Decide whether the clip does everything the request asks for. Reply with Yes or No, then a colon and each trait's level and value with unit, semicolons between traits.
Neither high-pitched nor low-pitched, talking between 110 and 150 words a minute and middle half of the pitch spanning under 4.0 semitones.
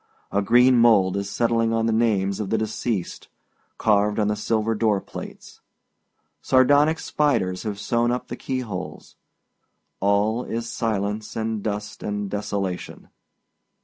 No: low, 110 Hz; average, 140 wpm; narrow, 2.5 semitones